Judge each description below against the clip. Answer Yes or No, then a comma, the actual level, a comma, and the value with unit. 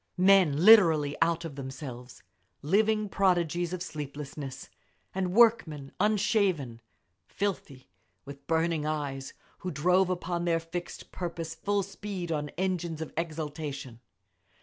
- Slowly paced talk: Yes, slow, 120 wpm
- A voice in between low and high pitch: Yes, medium, 165 Hz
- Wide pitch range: No, average, 4.1 semitones